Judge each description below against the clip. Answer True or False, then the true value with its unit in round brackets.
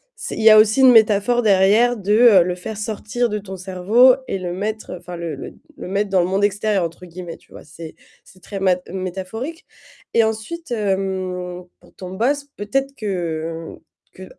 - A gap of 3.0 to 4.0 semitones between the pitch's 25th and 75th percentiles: True (3.4 semitones)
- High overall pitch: True (200 Hz)